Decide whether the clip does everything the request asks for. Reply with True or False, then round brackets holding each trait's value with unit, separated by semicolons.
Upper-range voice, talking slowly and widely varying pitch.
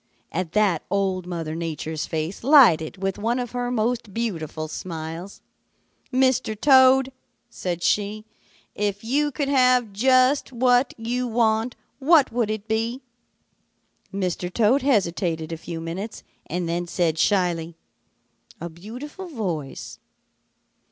True (210 Hz; 125 wpm; 6.4 semitones)